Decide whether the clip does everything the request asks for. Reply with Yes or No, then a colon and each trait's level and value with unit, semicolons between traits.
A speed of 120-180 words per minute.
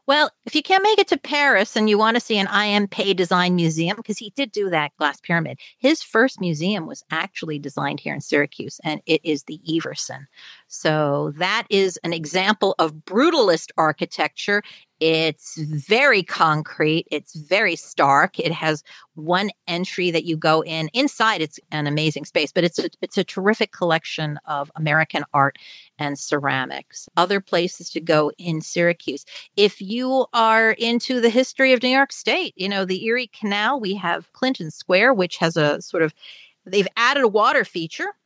Yes: average, 175 wpm